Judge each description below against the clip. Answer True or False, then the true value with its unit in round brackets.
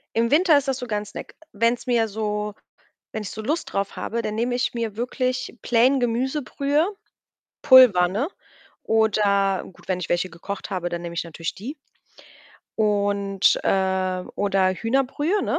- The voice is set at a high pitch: True (220 Hz)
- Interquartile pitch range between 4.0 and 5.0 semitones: True (4.4 semitones)